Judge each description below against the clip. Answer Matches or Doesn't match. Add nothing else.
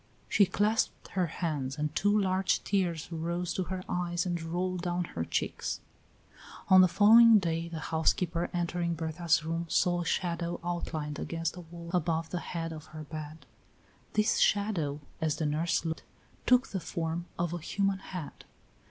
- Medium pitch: Matches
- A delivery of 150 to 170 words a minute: Matches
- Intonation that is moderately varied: Doesn't match